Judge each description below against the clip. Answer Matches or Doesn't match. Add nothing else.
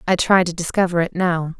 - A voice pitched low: Doesn't match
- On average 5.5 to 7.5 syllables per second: Matches